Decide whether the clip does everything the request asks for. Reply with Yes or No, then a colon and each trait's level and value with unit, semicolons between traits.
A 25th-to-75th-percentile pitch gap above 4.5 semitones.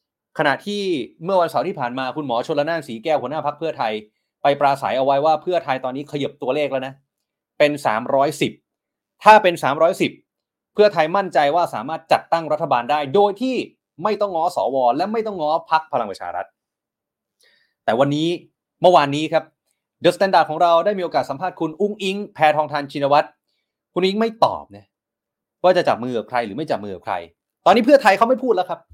Yes: average, 5.0 semitones